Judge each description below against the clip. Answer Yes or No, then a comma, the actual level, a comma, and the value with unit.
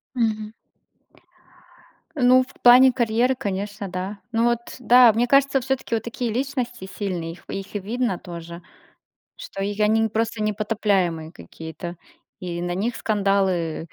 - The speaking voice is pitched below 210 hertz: No, high, 215 Hz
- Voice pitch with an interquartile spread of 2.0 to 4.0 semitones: No, average, 4.5 semitones